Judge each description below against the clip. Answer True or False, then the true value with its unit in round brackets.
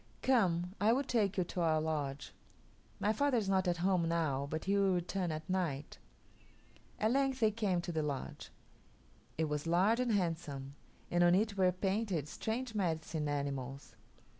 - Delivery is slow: False (170 wpm)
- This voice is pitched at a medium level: True (175 Hz)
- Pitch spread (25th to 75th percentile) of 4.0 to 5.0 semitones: True (4.7 semitones)